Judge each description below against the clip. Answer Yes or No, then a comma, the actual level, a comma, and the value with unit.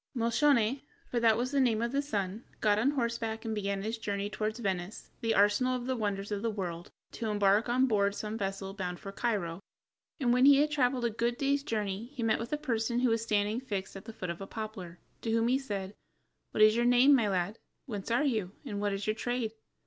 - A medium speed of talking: No, fast, 235 wpm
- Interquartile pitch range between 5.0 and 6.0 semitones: No, average, 3.2 semitones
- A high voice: Yes, high, 220 Hz